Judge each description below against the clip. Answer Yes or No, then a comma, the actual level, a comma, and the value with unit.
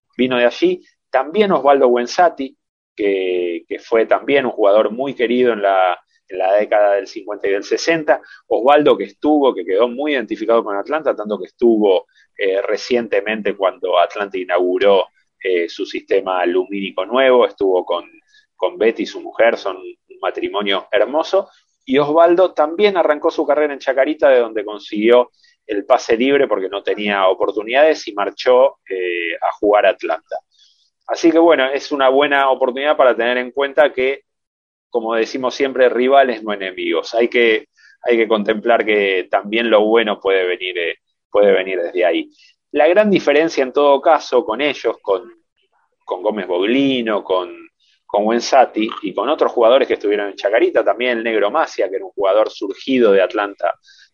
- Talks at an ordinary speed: Yes, average, 165 wpm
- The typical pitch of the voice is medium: Yes, medium, 165 Hz